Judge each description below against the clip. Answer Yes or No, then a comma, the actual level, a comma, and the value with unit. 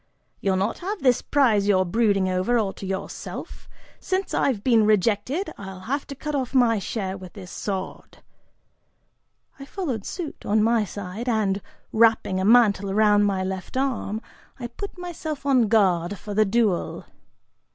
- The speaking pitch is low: No, high, 215 Hz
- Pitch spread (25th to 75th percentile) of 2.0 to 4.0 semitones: No, average, 4.6 semitones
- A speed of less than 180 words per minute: Yes, average, 160 wpm